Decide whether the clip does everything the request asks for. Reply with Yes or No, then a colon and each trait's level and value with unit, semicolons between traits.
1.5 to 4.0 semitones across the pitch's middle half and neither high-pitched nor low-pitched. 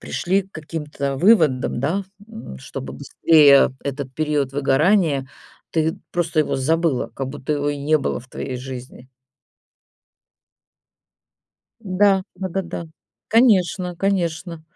No: average, 4.8 semitones; medium, 155 Hz